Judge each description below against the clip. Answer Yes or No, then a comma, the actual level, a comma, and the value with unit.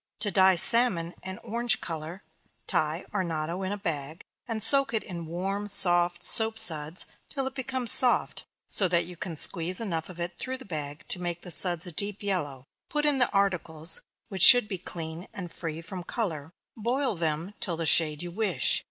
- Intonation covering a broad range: No, average, 4.3 semitones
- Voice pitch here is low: No, medium, 180 Hz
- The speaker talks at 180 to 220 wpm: Yes, average, 195 wpm